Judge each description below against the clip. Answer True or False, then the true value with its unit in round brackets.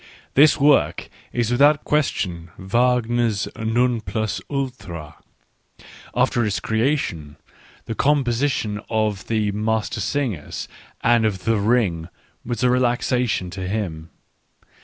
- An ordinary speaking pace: False (105 wpm)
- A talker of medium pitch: False (110 Hz)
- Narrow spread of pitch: False (4.0 semitones)